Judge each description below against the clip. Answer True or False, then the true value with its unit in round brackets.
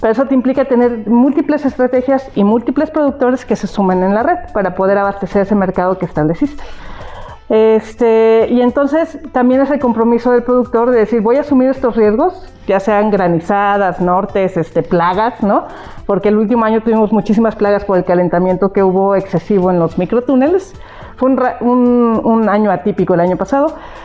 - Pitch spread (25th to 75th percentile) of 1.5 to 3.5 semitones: False (4.5 semitones)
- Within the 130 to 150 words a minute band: False (175 wpm)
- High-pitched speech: True (220 Hz)